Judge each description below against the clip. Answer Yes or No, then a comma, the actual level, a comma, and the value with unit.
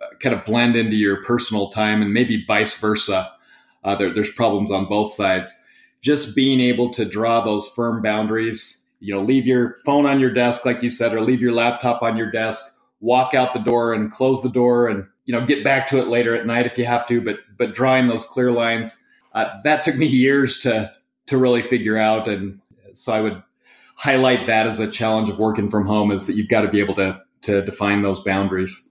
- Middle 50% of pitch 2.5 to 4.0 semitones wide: Yes, average, 2.8 semitones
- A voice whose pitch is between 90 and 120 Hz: Yes, low, 115 Hz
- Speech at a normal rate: No, fast, 220 wpm